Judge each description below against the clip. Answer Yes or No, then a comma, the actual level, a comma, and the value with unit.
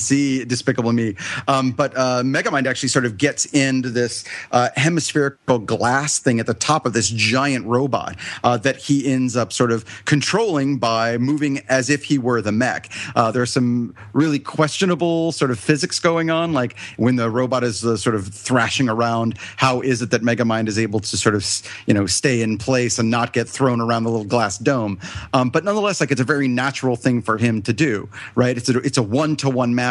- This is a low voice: Yes, low, 125 Hz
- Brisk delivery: Yes, fast, 215 wpm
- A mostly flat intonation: No, average, 3.0 semitones